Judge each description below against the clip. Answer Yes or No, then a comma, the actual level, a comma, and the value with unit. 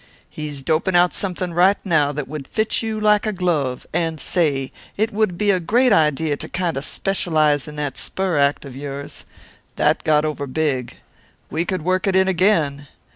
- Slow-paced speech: No, average, 185 wpm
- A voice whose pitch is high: No, medium, 160 Hz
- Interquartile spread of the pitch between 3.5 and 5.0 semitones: Yes, average, 4.5 semitones